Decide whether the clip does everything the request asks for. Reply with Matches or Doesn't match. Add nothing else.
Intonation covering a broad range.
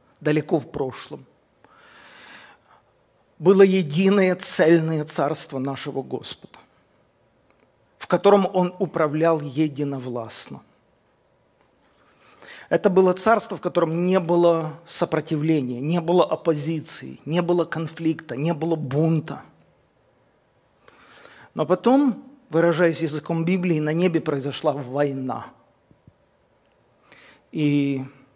Doesn't match